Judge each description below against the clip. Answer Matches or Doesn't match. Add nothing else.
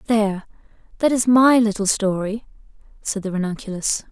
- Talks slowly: Matches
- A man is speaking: Doesn't match